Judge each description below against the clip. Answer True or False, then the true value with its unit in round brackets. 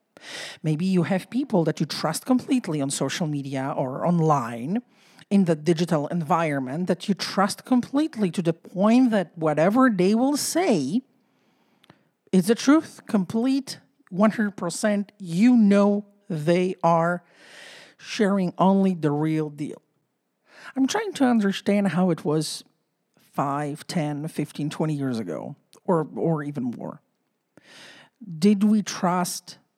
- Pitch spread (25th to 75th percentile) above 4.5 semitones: True (5.2 semitones)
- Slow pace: True (125 wpm)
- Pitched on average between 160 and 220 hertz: True (185 Hz)